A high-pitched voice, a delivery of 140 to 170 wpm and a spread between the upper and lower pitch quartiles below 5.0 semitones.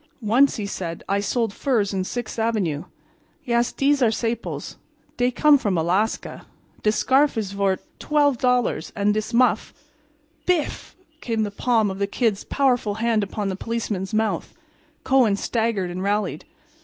Yes: high, 220 Hz; average, 150 wpm; average, 3.5 semitones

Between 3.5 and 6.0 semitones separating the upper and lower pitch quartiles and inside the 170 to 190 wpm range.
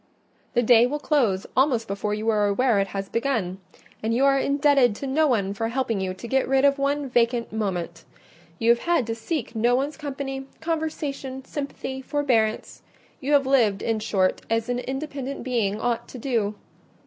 Yes: average, 4.0 semitones; average, 185 wpm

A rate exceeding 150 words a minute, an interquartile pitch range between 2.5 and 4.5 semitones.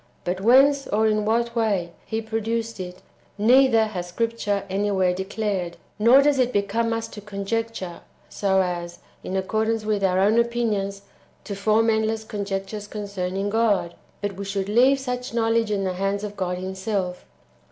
Yes: average, 160 wpm; average, 2.8 semitones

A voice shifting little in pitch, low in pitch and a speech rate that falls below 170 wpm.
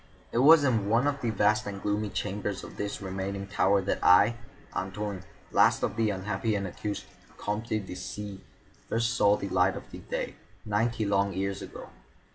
No: narrow, 1.9 semitones; low, 105 Hz; average, 175 wpm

